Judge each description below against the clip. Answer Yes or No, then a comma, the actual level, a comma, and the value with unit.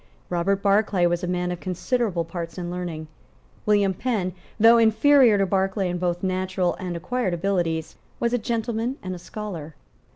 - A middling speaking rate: Yes, average, 165 wpm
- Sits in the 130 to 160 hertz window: No, medium, 185 Hz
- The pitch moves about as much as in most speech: Yes, average, 3.5 semitones